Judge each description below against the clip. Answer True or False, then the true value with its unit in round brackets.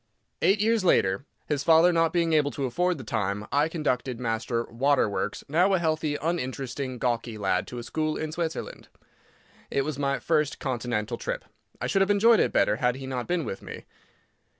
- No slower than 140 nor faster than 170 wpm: False (185 wpm)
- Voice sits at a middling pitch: True (145 Hz)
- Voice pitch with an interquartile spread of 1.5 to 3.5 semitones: False (5.4 semitones)